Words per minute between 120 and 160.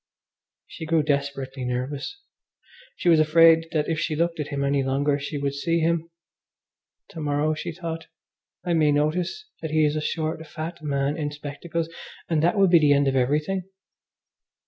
No: average, 175 wpm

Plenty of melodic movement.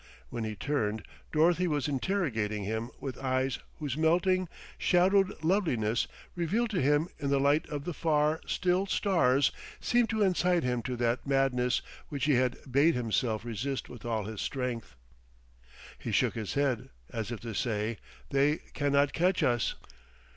Yes: wide, 5.8 semitones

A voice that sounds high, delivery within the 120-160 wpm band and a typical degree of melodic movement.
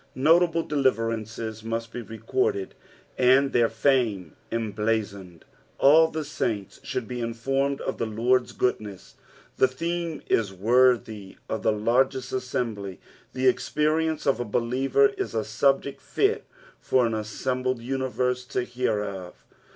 No: low, 125 Hz; slow, 135 wpm; average, 3.5 semitones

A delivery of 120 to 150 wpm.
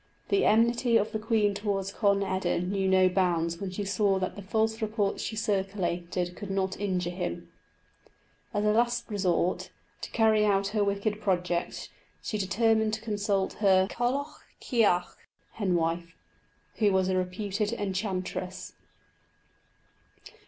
Yes: average, 140 wpm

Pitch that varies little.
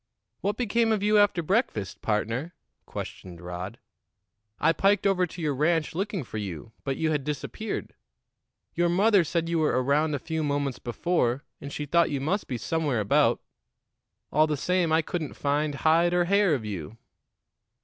No: average, 5.0 semitones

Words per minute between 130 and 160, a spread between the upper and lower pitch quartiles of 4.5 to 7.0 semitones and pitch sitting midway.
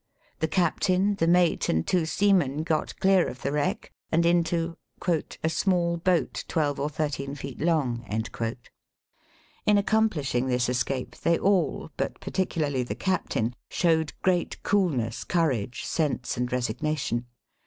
Yes: average, 140 wpm; average, 5.3 semitones; medium, 160 Hz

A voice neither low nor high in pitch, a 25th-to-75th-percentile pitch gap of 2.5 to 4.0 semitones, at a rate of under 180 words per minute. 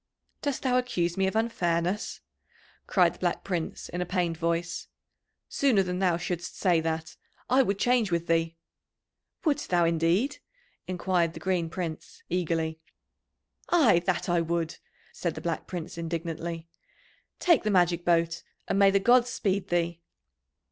Yes: medium, 175 Hz; average, 2.9 semitones; average, 150 wpm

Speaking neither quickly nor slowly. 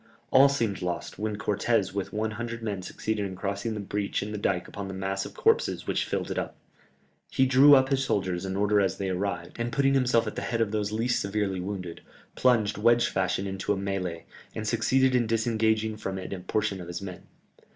No: fast, 215 wpm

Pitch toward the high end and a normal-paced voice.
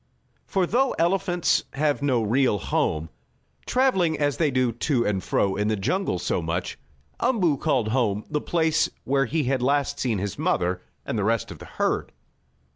No: low, 135 Hz; average, 175 wpm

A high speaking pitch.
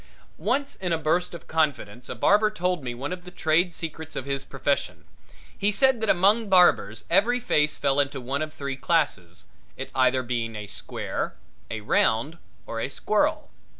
No: medium, 155 Hz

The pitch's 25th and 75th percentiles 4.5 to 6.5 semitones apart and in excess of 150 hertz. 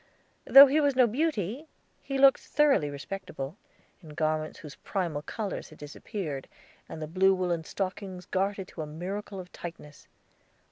Yes: average, 5.3 semitones; medium, 185 Hz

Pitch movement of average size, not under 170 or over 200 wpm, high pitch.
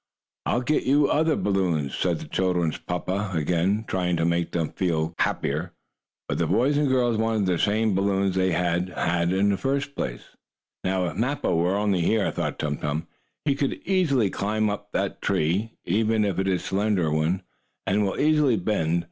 No: average, 4.4 semitones; average, 175 wpm; very low, 95 Hz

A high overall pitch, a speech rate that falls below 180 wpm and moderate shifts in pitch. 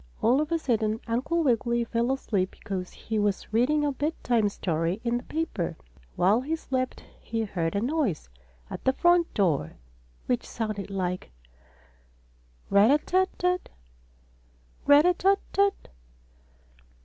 No: high, 235 Hz; average, 150 wpm; wide, 6.9 semitones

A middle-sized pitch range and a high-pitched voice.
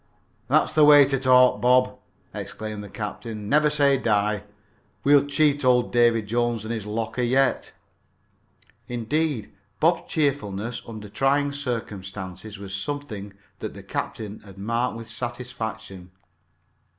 No: average, 4.5 semitones; low, 120 Hz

